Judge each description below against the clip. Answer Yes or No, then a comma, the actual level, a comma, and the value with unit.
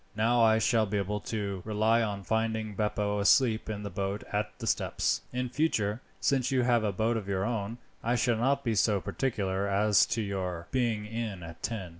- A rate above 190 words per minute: Yes, average, 200 wpm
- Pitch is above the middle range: No, low, 110 Hz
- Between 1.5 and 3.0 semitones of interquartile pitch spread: Yes, narrow, 2.5 semitones